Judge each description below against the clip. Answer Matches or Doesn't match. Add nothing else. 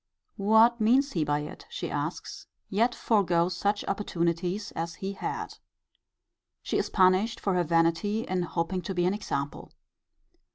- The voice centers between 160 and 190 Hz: Matches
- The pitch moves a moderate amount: Matches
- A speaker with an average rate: Matches